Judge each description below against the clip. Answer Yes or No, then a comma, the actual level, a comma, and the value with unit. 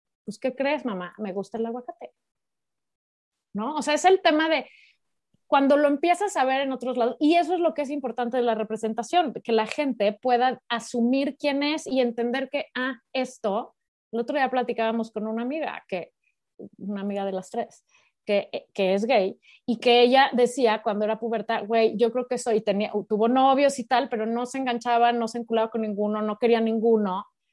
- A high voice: Yes, high, 240 Hz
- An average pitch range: Yes, average, 3.3 semitones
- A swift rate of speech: Yes, fast, 200 wpm